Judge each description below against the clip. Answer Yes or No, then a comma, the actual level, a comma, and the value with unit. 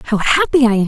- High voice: Yes, high, 215 Hz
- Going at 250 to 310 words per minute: Yes, fast, 275 wpm